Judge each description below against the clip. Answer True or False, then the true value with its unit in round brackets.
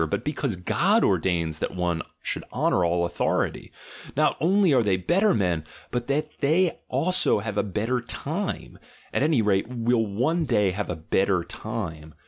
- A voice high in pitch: False (110 Hz)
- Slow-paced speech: False (170 wpm)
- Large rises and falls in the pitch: True (8.5 semitones)